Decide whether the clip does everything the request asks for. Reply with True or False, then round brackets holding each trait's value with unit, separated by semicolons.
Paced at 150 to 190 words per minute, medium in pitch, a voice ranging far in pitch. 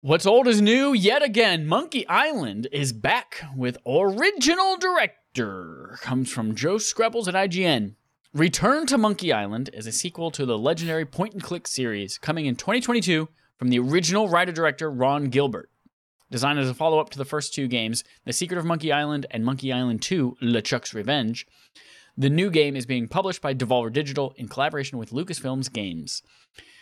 True (170 wpm; 145 Hz; 5.9 semitones)